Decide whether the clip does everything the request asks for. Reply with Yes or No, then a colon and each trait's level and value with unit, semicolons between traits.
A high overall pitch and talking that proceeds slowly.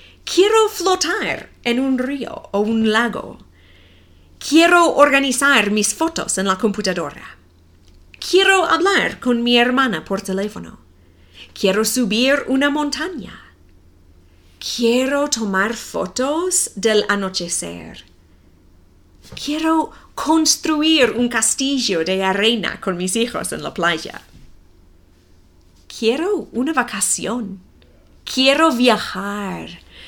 Yes: high, 220 Hz; slow, 95 wpm